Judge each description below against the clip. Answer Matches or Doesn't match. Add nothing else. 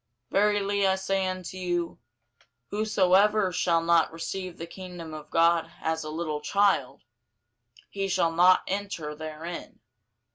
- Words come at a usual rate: Doesn't match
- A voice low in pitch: Doesn't match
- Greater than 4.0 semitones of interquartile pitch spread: Doesn't match